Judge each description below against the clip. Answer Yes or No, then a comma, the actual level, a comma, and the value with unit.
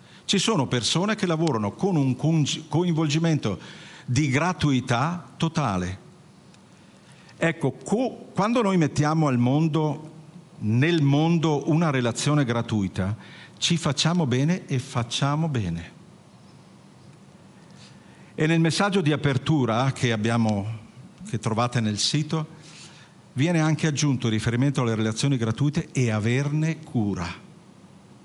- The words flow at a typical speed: No, slow, 110 wpm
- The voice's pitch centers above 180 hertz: No, medium, 150 Hz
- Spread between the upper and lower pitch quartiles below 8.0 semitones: Yes, average, 5.1 semitones